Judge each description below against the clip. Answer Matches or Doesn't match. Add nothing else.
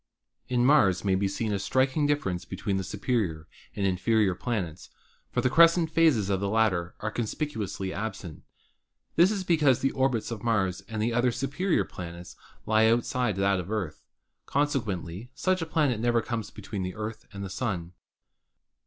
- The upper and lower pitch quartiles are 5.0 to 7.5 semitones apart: Matches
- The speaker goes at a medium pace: Matches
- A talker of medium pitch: Doesn't match